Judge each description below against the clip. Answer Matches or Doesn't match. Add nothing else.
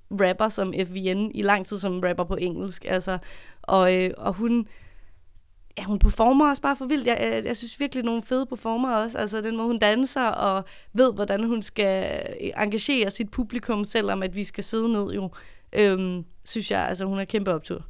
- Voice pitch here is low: Doesn't match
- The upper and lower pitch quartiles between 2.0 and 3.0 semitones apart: Doesn't match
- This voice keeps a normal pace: Matches